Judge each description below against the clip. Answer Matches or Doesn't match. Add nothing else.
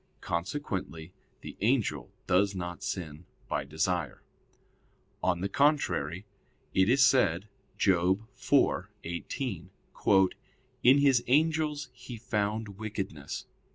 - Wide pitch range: Matches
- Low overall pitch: Matches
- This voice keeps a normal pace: Doesn't match